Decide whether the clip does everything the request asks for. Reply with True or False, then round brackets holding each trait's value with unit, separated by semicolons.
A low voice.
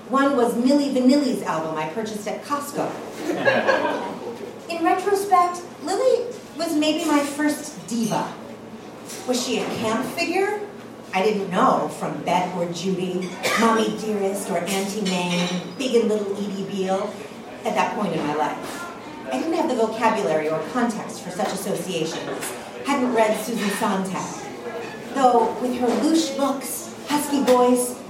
False (230 Hz)